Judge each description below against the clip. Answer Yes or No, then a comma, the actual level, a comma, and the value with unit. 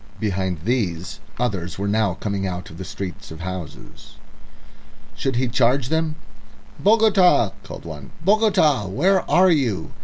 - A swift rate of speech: No, average, 140 wpm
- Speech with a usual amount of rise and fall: No, wide, 8.9 semitones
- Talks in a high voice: No, low, 110 Hz